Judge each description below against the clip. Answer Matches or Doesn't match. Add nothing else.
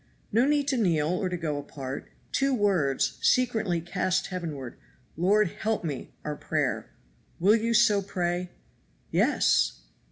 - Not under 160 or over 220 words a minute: Doesn't match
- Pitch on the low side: Doesn't match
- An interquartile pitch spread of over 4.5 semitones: Matches